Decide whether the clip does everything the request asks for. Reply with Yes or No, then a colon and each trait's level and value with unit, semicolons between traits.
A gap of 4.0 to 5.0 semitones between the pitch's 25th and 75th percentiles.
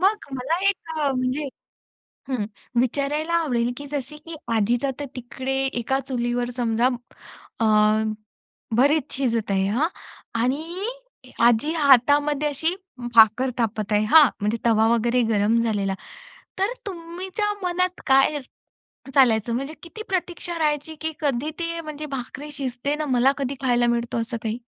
Yes: average, 4.6 semitones